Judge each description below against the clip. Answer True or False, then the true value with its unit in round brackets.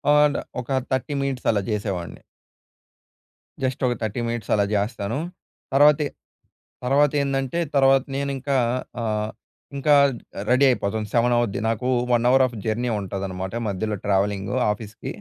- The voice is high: False (120 Hz)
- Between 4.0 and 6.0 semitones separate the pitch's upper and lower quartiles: True (4.6 semitones)